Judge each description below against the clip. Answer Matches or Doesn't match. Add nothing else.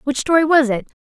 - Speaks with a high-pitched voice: Matches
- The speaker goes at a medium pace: Doesn't match